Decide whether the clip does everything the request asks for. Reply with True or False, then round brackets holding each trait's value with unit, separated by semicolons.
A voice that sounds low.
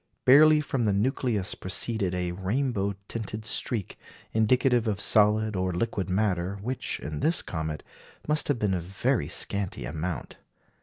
True (105 Hz)